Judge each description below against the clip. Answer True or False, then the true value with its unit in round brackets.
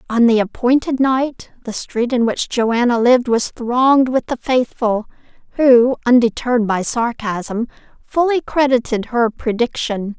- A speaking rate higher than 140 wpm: False (135 wpm)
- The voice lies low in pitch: False (240 Hz)